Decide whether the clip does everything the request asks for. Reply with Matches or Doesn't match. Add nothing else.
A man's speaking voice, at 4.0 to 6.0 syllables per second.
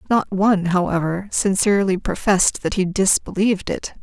Doesn't match